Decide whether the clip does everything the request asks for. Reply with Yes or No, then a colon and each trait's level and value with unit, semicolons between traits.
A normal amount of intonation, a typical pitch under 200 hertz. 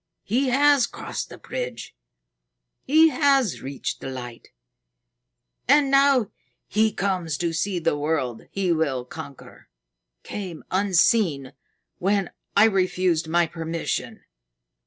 No: wide, 6.8 semitones; medium, 185 Hz